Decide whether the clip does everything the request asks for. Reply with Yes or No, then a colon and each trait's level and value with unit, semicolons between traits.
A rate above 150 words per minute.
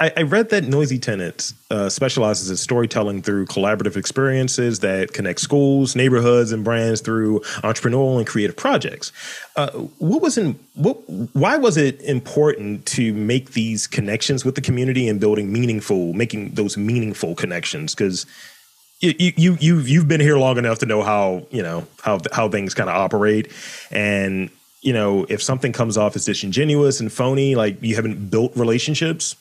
Yes: average, 165 wpm